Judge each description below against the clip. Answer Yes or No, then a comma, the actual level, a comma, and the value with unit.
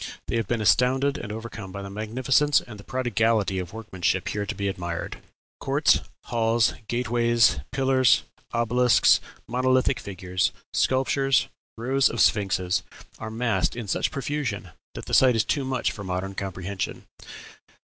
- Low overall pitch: Yes, low, 115 Hz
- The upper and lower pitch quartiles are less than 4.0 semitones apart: No, average, 4.3 semitones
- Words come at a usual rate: Yes, average, 150 wpm